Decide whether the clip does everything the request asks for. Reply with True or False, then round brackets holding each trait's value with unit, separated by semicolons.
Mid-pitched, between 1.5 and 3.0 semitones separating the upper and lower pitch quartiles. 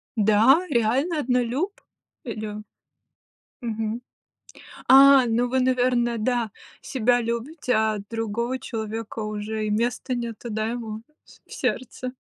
False (235 Hz; 2.6 semitones)